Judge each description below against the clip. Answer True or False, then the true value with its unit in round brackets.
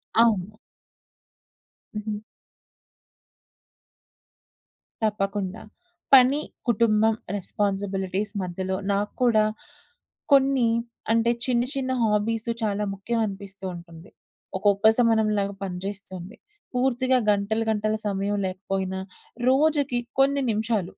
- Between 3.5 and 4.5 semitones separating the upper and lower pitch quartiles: False (3.0 semitones)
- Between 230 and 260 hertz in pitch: False (210 Hz)